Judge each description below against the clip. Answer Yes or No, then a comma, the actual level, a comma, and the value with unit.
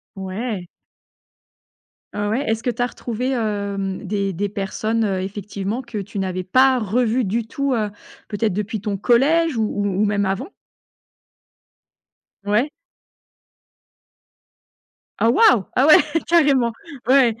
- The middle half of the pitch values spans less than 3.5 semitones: No, average, 3.8 semitones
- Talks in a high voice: Yes, high, 215 Hz